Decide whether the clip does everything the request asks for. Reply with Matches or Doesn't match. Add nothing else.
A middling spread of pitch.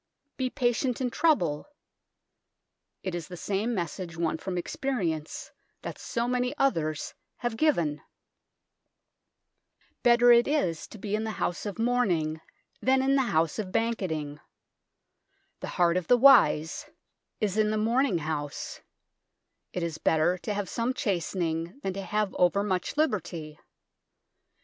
Doesn't match